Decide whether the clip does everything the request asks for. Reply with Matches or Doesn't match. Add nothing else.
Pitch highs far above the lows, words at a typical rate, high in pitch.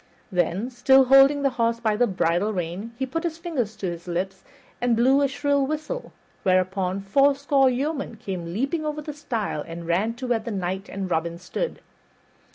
Matches